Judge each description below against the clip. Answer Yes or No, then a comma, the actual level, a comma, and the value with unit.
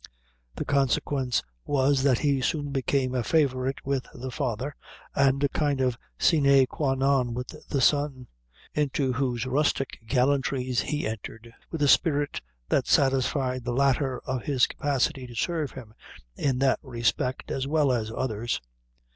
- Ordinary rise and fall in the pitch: No, narrow, 2.0 semitones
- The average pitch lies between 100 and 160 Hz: Yes, low, 135 Hz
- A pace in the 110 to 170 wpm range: Yes, average, 150 wpm